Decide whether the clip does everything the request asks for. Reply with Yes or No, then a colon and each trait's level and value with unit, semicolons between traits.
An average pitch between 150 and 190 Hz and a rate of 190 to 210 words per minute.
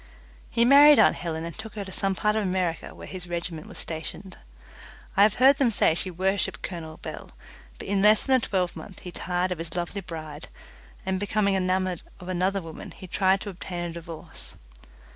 Yes: medium, 185 Hz; average, 200 wpm